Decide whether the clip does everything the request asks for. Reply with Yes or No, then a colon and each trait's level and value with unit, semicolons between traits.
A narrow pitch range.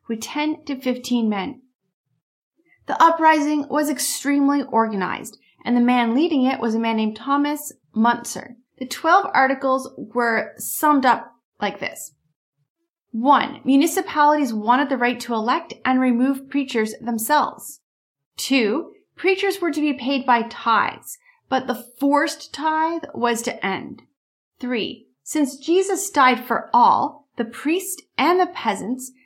No: average, 4.0 semitones